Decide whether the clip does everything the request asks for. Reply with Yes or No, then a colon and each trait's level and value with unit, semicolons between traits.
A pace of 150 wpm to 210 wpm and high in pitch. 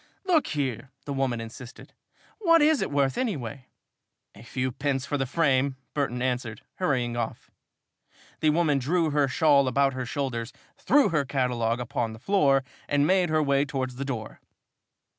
No: average, 160 wpm; low, 135 Hz